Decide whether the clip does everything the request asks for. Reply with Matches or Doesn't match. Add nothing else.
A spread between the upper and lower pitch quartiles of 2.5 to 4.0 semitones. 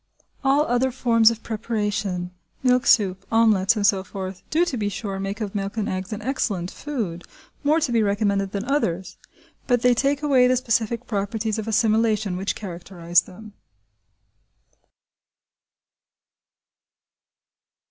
Matches